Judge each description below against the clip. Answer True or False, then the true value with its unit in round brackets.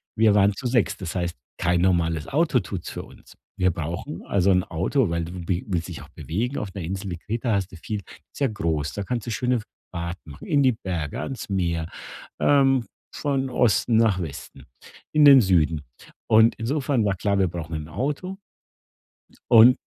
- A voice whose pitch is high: False (100 Hz)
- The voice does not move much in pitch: False (6.3 semitones)